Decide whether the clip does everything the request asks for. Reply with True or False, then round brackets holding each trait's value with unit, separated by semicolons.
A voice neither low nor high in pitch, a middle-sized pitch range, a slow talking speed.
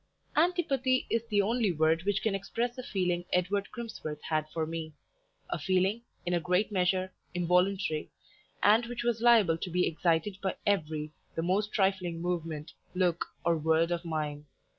False (180 Hz; 4.2 semitones; 160 wpm)